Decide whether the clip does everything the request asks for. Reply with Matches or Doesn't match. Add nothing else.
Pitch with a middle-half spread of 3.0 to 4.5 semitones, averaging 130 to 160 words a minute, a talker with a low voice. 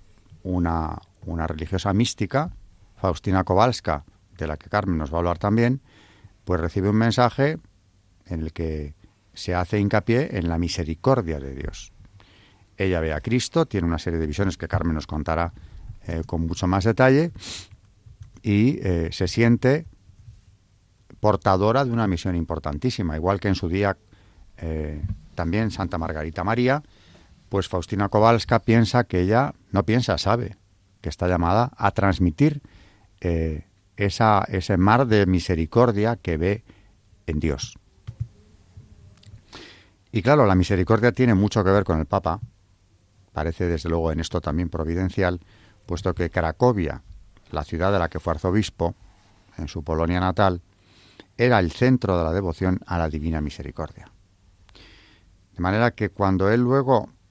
Matches